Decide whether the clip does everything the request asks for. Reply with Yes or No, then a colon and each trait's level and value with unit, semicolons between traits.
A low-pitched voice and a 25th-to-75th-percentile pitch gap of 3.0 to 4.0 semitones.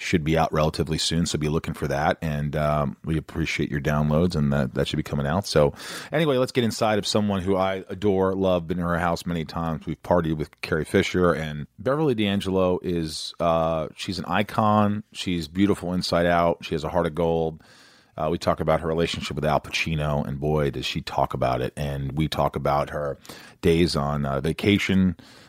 Yes: very low, 80 Hz; average, 3.7 semitones